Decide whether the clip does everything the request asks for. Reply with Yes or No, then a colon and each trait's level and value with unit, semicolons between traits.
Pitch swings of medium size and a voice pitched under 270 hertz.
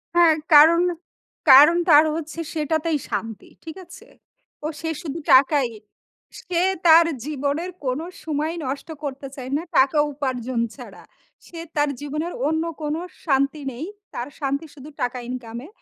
No: average, 3.1 semitones; very high, 295 Hz